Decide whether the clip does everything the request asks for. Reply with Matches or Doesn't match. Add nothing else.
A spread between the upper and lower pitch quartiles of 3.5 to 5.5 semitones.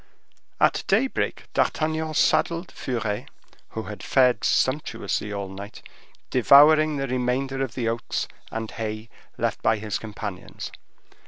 Matches